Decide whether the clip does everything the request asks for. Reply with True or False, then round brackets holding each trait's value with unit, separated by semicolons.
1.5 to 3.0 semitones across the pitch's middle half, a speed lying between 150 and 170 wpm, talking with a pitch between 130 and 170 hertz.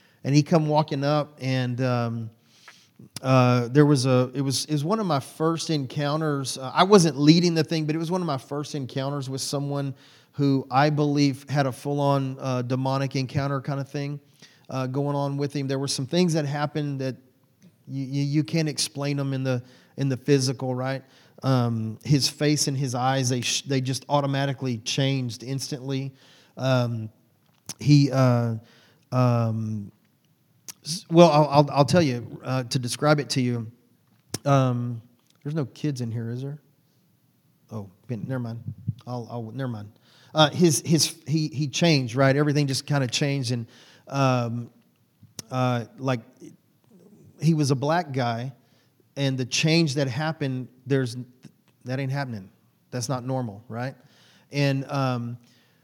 True (2.7 semitones; 160 wpm; 135 Hz)